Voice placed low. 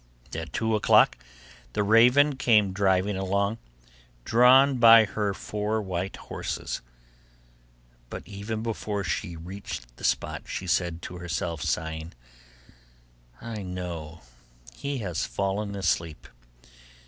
Yes: low, 100 Hz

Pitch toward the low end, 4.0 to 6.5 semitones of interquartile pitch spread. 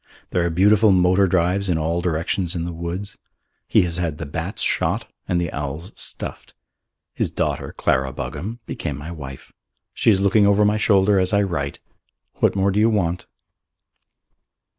No: very low, 90 Hz; average, 3.2 semitones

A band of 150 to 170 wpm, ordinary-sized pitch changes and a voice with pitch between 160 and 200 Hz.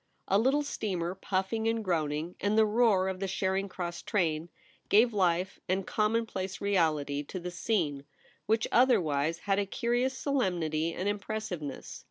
Yes: average, 160 wpm; average, 4.2 semitones; high, 190 Hz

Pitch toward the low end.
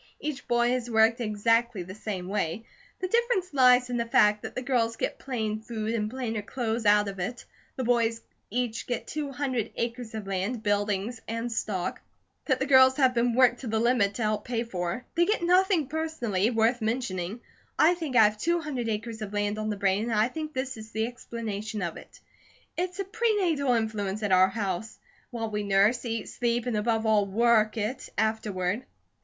No: high, 230 Hz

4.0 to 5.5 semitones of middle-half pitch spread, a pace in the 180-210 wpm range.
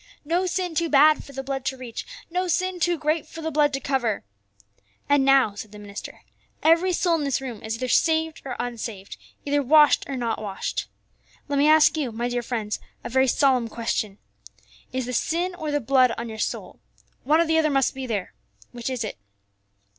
Yes: average, 4.7 semitones; fast, 205 wpm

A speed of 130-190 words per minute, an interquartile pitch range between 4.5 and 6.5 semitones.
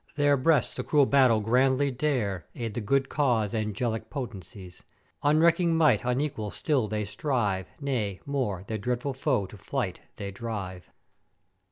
Yes: average, 145 wpm; average, 5.2 semitones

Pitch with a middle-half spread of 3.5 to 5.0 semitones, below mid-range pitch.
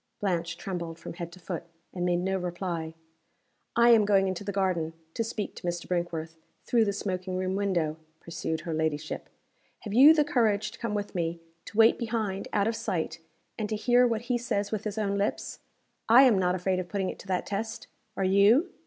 No: average, 3.8 semitones; high, 195 Hz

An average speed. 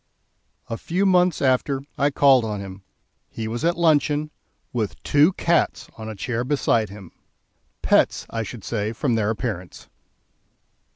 Yes: average, 150 wpm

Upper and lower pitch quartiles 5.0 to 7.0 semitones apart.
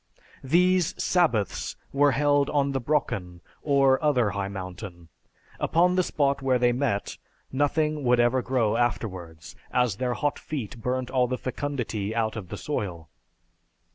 Yes: wide, 5.4 semitones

